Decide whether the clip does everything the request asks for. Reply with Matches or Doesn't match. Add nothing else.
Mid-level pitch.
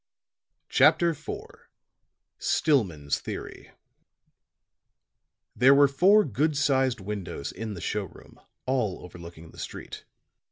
Doesn't match